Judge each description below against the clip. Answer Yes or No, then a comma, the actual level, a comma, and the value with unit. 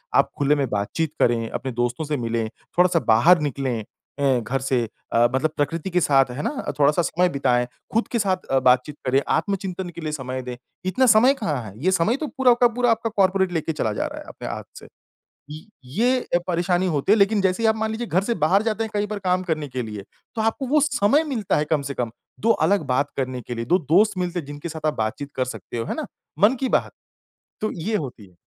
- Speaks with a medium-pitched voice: Yes, medium, 160 Hz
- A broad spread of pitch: Yes, wide, 7.5 semitones